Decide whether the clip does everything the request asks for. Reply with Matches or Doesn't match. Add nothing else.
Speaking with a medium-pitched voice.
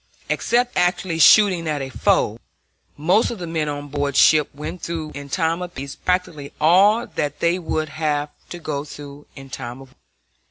Matches